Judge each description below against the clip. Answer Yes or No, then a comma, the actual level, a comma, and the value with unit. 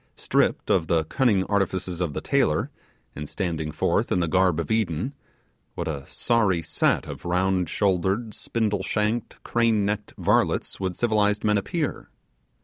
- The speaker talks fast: No, average, 150 wpm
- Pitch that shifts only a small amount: No, average, 3.7 semitones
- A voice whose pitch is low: Yes, very low, 95 Hz